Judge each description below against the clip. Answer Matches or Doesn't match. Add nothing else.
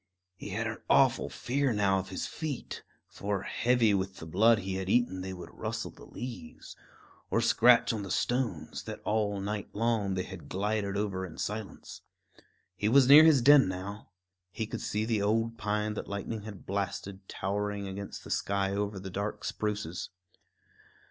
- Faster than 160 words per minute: Matches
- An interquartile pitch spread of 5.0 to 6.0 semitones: Doesn't match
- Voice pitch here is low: Matches